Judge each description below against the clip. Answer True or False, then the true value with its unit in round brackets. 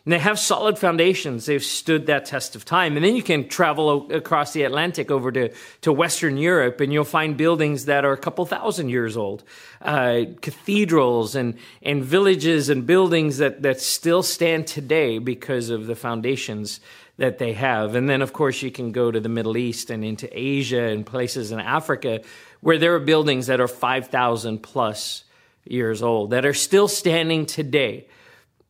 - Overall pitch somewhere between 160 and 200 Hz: False (140 Hz)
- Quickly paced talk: False (185 wpm)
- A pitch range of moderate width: True (4.8 semitones)